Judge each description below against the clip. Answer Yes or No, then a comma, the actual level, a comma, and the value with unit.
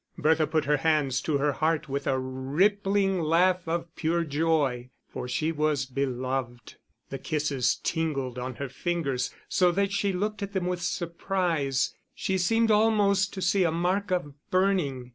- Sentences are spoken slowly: No, average, 160 wpm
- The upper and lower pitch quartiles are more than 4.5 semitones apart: Yes, average, 5.2 semitones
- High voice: No, medium, 160 Hz